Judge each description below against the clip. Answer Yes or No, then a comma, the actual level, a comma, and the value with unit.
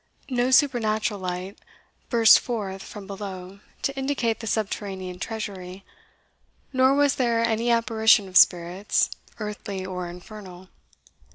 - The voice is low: No, high, 210 Hz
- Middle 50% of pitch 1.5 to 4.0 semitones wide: Yes, average, 3.6 semitones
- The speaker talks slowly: Yes, slow, 115 wpm